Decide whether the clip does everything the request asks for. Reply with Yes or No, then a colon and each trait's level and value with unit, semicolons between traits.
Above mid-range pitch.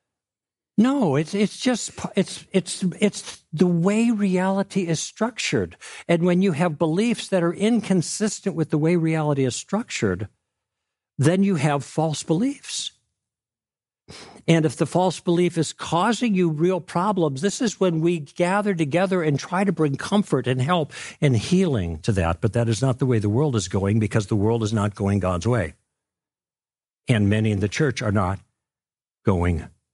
No: medium, 160 Hz